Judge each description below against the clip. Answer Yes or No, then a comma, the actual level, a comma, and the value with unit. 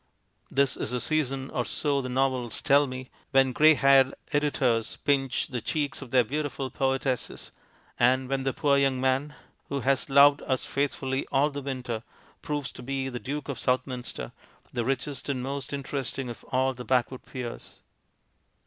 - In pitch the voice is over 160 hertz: No, low, 135 Hz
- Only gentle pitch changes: Yes, narrow, 1.6 semitones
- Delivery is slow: No, average, 165 wpm